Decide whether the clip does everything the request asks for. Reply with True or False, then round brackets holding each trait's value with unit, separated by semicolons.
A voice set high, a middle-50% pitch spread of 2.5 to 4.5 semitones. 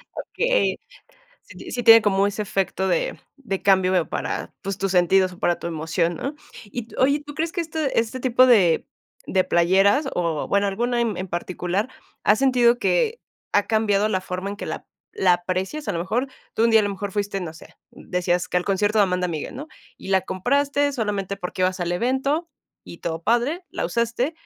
False (200 Hz; 5.0 semitones)